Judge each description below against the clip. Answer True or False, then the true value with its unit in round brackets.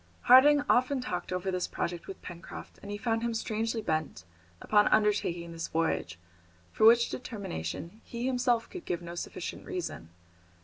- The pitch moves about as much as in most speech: False (5.8 semitones)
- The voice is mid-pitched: False (210 Hz)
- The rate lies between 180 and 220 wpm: False (160 wpm)